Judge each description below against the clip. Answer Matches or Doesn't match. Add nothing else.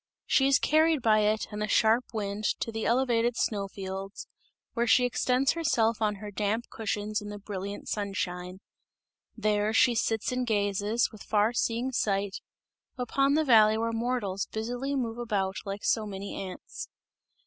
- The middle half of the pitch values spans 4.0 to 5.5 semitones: Doesn't match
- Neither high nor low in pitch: Doesn't match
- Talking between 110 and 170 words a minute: Matches